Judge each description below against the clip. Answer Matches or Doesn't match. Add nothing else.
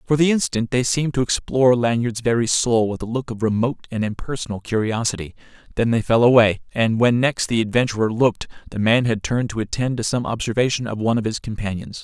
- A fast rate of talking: Matches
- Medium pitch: Doesn't match